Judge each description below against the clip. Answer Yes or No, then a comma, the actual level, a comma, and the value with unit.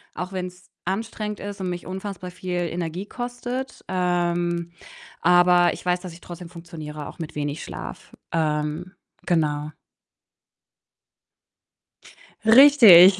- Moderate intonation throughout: No, narrow, 2.1 semitones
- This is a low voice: No, medium, 180 Hz